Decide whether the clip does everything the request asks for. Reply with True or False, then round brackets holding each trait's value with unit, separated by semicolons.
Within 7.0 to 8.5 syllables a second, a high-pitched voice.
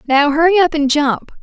False (5.5 syllables/s; 300 Hz)